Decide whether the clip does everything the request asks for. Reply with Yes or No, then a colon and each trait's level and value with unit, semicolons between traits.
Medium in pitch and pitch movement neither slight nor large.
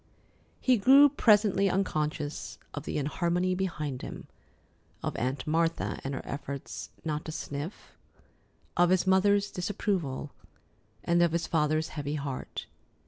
Yes: medium, 165 Hz; average, 4.4 semitones